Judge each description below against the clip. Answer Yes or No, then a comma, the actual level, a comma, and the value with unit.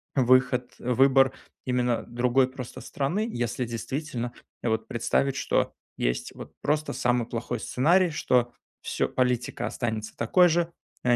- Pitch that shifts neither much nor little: No, narrow, 2.2 semitones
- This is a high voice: No, low, 125 Hz